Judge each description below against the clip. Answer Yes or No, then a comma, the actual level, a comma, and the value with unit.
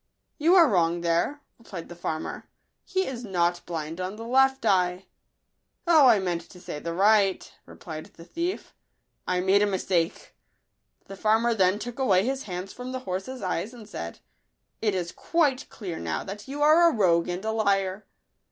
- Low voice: No, high, 195 Hz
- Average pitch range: No, wide, 5.9 semitones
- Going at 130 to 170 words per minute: No, average, 195 wpm